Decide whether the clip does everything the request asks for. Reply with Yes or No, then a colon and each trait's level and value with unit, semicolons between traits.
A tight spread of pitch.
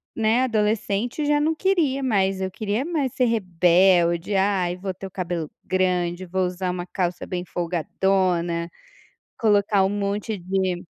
No: average, 3.3 semitones